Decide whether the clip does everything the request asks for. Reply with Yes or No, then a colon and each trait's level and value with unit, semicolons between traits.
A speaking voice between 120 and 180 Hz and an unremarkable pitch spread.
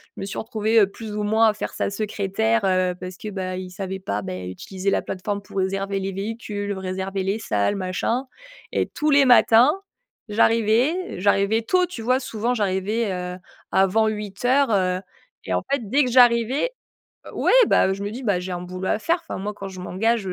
No: high, 205 Hz; average, 3.2 semitones